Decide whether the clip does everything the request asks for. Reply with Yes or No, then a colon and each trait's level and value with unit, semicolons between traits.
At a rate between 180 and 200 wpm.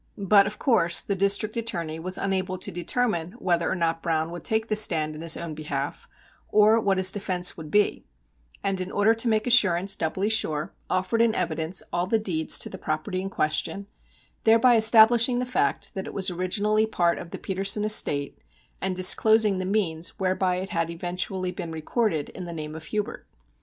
Yes: average, 190 wpm